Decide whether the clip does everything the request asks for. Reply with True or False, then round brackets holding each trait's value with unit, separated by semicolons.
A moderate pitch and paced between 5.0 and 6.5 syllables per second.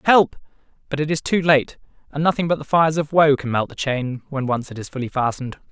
True (145 Hz; 6.1 syllables/s)